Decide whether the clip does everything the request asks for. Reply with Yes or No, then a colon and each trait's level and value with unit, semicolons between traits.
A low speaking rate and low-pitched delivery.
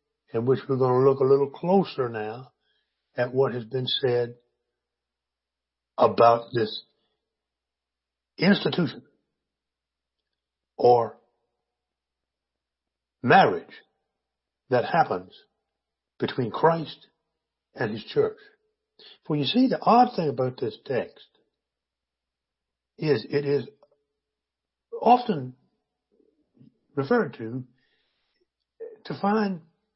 Yes: slow, 90 wpm; low, 125 Hz